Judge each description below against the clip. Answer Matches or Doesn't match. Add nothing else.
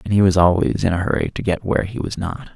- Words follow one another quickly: Matches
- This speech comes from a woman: Doesn't match